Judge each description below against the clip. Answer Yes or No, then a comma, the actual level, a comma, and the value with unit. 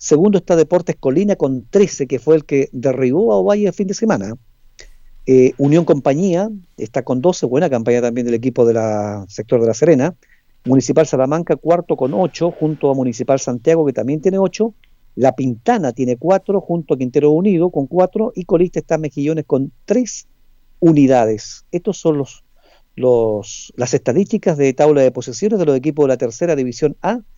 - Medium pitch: Yes, medium, 150 Hz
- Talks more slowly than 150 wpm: No, average, 180 wpm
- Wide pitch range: Yes, wide, 5.8 semitones